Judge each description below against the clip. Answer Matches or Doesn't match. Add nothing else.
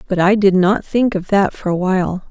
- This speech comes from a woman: Matches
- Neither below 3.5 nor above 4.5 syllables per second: Doesn't match